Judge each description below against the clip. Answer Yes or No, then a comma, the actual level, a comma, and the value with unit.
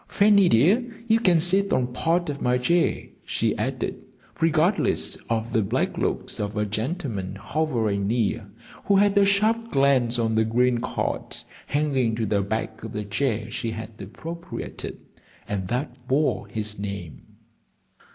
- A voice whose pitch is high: No, low, 125 Hz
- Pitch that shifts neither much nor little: No, wide, 7.4 semitones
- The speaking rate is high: No, average, 150 wpm